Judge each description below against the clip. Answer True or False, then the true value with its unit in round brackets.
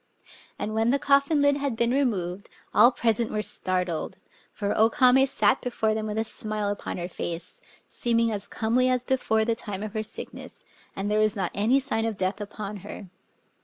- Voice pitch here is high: True (220 Hz)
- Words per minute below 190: False (195 wpm)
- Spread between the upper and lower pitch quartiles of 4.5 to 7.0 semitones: False (3.3 semitones)